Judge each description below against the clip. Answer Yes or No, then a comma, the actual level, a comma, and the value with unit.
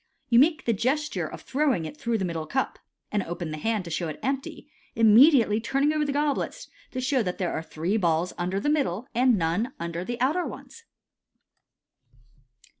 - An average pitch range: No, wide, 7.7 semitones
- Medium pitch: No, high, 230 Hz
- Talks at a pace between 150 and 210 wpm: Yes, average, 190 wpm